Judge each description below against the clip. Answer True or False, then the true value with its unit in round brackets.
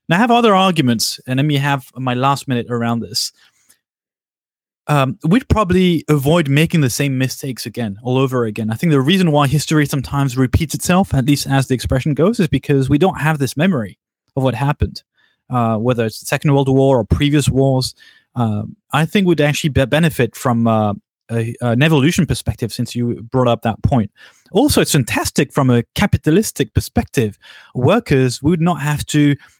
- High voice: False (135 Hz)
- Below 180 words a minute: False (185 wpm)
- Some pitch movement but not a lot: True (3.8 semitones)